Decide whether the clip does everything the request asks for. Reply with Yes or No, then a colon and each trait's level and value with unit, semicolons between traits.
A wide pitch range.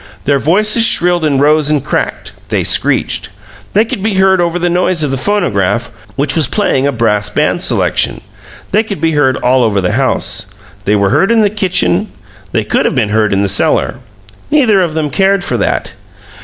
Yes: wide, 7.2 semitones